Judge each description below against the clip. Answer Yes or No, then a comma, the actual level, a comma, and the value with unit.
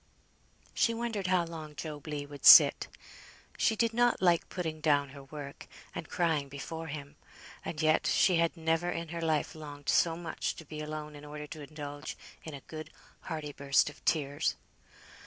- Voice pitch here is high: No, medium, 155 Hz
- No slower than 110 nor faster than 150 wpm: No, average, 175 wpm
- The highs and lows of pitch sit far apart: No, narrow, 2.4 semitones